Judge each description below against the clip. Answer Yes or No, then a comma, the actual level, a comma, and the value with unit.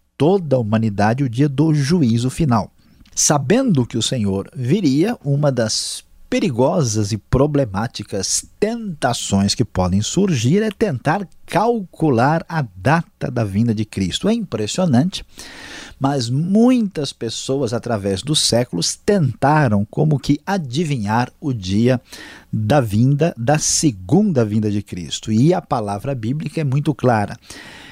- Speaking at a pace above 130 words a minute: No, average, 125 wpm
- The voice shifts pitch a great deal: Yes, wide, 6.3 semitones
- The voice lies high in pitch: No, low, 135 Hz